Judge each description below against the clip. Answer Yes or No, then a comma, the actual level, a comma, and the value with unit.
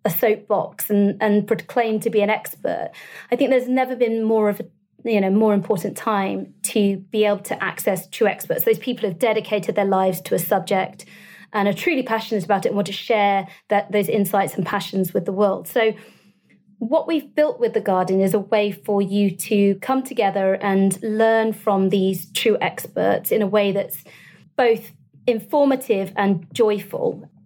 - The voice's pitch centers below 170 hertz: No, high, 210 Hz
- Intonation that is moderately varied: No, narrow, 2.3 semitones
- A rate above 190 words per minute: No, average, 185 wpm